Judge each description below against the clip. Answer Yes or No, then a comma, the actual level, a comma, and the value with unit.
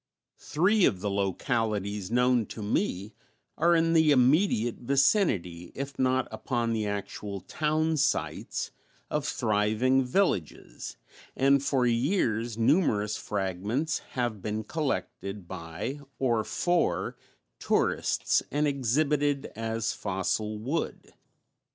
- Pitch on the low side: Yes, low, 120 Hz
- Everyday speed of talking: No, slow, 105 wpm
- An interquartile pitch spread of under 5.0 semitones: No, wide, 5.5 semitones